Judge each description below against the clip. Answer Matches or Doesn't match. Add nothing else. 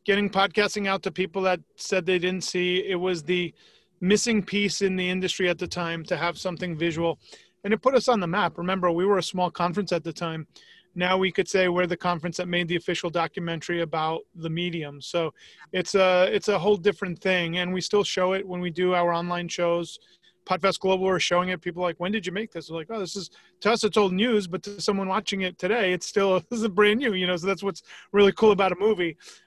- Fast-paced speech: Matches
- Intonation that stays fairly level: Matches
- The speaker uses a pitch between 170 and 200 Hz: Matches